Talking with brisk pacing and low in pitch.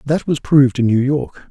Yes: fast, 240 wpm; low, 130 Hz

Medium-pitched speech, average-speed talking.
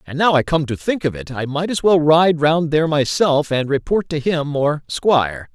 No: medium, 150 Hz; fast, 240 wpm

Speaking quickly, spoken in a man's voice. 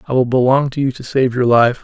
Yes: fast, 295 wpm; male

